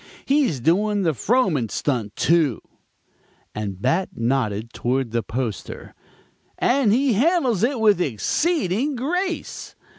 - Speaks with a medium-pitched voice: Yes, medium, 175 Hz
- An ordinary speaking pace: No, slow, 115 wpm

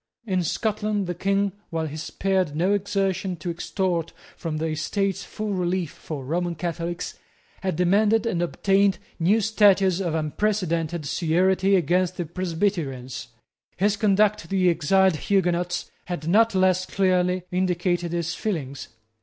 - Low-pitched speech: No, medium, 180 Hz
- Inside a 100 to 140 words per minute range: Yes, slow, 135 wpm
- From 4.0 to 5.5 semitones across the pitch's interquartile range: No, average, 2.7 semitones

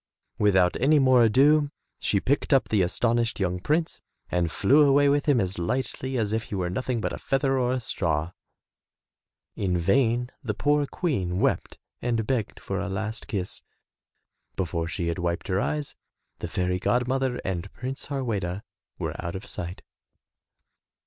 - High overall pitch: No, low, 115 Hz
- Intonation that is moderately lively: No, wide, 6.4 semitones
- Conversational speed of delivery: Yes, average, 170 wpm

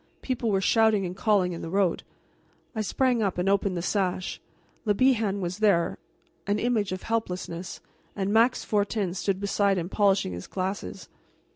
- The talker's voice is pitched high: Yes, high, 200 Hz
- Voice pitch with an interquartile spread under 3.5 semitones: Yes, average, 2.8 semitones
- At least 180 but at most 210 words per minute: No, average, 165 wpm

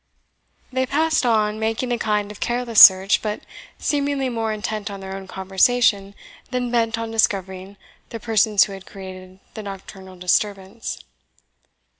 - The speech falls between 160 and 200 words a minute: No, average, 145 wpm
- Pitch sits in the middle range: No, high, 210 Hz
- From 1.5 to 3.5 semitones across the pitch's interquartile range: Yes, average, 3.2 semitones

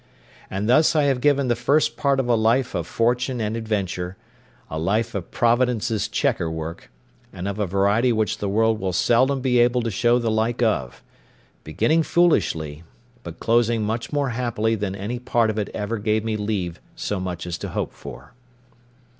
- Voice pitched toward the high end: No, low, 110 Hz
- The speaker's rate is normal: Yes, average, 180 wpm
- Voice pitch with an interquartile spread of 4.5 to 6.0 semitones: No, average, 3.7 semitones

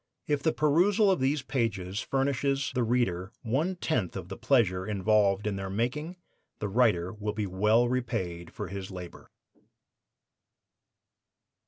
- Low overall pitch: Yes, low, 115 Hz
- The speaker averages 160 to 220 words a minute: No, average, 140 wpm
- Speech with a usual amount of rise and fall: No, wide, 6.0 semitones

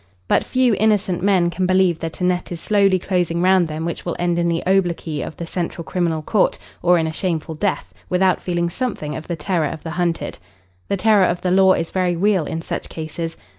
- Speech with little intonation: Yes, narrow, 2.2 semitones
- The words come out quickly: Yes, fast, 220 wpm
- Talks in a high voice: No, medium, 175 Hz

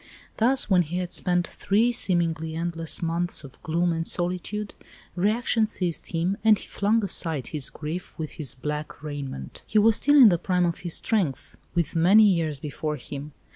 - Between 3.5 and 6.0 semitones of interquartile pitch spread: Yes, average, 4.3 semitones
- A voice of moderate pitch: Yes, medium, 175 Hz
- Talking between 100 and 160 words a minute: No, average, 175 wpm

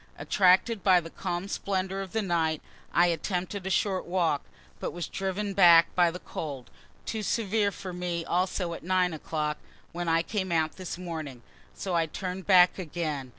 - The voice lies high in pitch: No, medium, 180 Hz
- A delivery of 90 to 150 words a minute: No, average, 175 wpm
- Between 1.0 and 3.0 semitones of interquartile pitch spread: Yes, narrow, 2.4 semitones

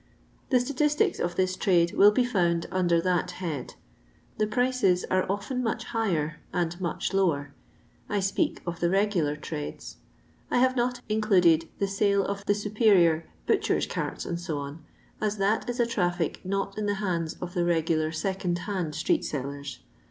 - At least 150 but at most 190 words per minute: Yes, average, 160 wpm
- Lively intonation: No, average, 3.7 semitones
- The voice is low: No, medium, 185 Hz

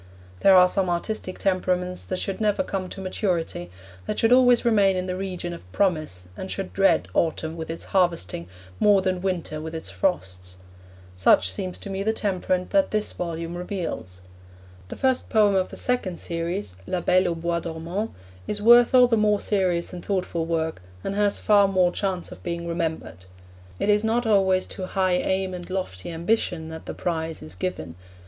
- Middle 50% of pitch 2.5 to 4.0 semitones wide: Yes, average, 3.1 semitones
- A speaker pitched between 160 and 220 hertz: Yes, medium, 185 Hz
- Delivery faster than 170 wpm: Yes, average, 185 wpm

